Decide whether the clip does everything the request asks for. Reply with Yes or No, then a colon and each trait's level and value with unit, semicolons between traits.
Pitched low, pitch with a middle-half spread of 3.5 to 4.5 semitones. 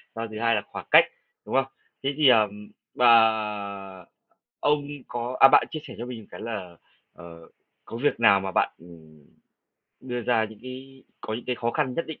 Yes: low, 115 Hz; average, 4.1 semitones